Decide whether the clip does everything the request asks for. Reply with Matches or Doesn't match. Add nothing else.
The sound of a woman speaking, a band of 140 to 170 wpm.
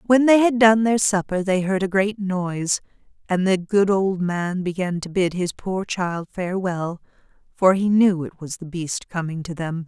Doesn't match